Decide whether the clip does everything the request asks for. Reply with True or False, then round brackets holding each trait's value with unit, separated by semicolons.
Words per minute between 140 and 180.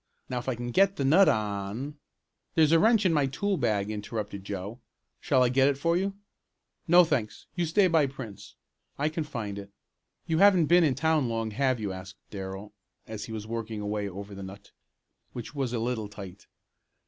False (200 wpm)